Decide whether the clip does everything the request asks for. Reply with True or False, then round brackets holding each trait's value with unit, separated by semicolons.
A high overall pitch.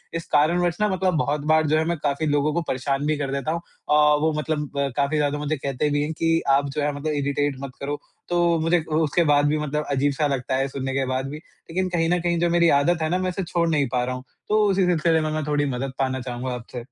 False (150 Hz)